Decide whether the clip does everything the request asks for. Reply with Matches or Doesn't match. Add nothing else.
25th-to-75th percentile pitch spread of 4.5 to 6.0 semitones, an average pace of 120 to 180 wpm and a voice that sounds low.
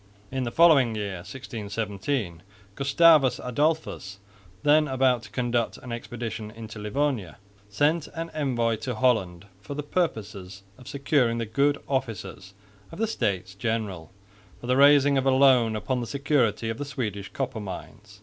Matches